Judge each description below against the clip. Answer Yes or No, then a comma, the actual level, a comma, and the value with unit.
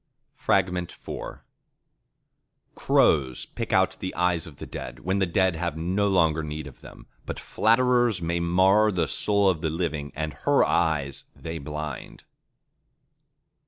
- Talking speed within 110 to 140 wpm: Yes, slow, 135 wpm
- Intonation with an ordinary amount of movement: Yes, average, 3.6 semitones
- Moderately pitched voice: No, very low, 85 Hz